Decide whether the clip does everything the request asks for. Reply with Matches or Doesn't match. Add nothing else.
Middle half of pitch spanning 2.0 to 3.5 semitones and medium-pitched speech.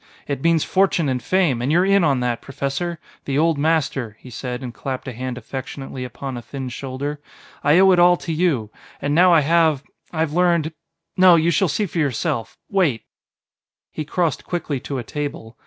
Doesn't match